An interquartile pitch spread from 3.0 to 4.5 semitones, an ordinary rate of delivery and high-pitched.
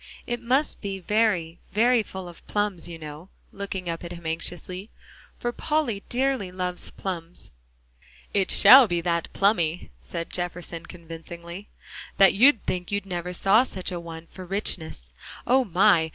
No: average, 3.5 semitones; average, 150 wpm; medium, 180 Hz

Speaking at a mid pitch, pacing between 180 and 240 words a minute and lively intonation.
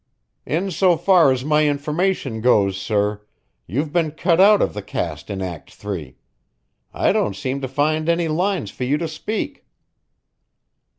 No: medium, 145 Hz; average, 160 wpm; wide, 8.3 semitones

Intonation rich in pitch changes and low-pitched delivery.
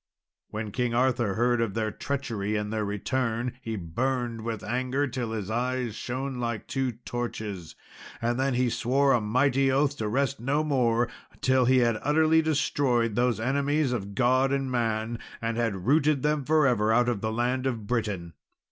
No: average, 3.0 semitones; low, 120 Hz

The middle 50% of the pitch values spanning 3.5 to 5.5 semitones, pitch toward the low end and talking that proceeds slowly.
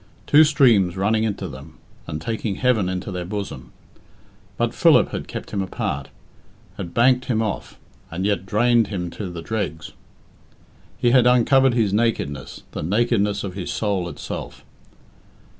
No: average, 4.7 semitones; low, 100 Hz; average, 150 wpm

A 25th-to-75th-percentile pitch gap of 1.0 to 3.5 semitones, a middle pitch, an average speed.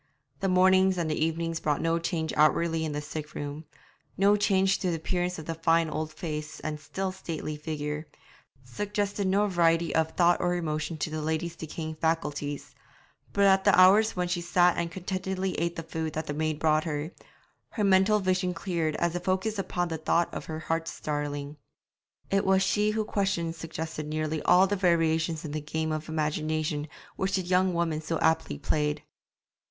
Yes: average, 3.0 semitones; medium, 165 Hz; average, 185 wpm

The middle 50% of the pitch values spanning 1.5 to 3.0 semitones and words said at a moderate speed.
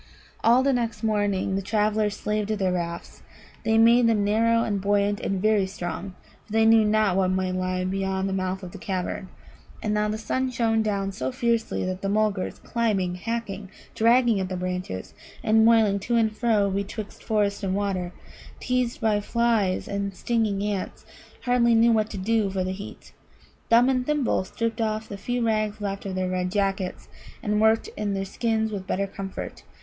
Yes: average, 2.7 semitones; average, 185 wpm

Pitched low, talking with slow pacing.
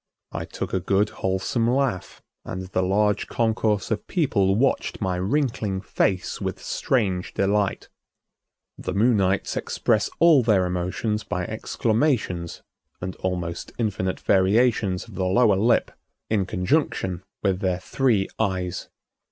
Yes: low, 100 Hz; slow, 125 wpm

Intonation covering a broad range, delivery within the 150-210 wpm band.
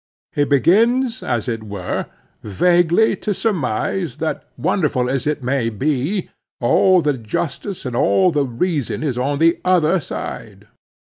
No: wide, 6.4 semitones; average, 140 wpm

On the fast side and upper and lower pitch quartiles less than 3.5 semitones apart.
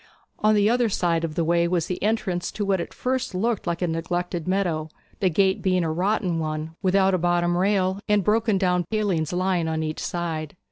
Yes: fast, 215 wpm; average, 2.9 semitones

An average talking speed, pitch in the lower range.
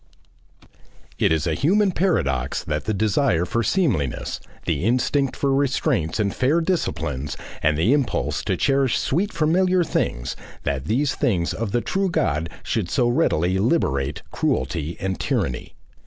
Yes: average, 145 wpm; low, 110 Hz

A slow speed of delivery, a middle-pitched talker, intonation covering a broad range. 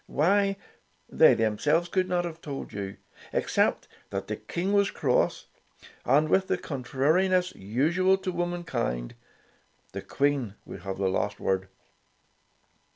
Yes: slow, 130 wpm; medium, 155 Hz; wide, 8.2 semitones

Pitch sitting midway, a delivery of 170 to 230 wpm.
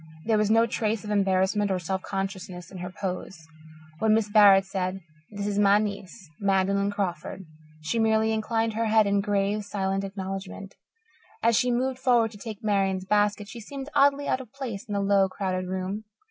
No: high, 205 Hz; average, 185 wpm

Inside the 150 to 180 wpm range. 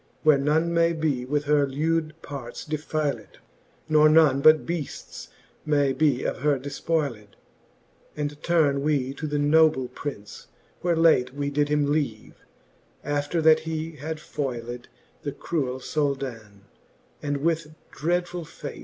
No: slow, 135 wpm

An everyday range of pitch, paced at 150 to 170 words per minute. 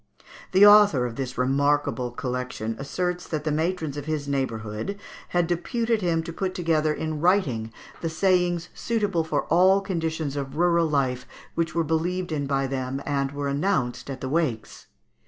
Yes: average, 4.5 semitones; average, 165 wpm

